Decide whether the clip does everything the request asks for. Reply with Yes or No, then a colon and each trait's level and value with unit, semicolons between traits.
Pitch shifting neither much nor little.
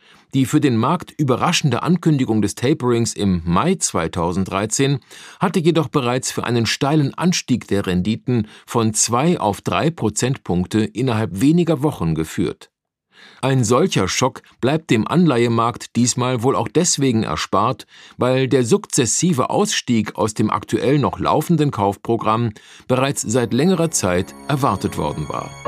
No: wide, 5.9 semitones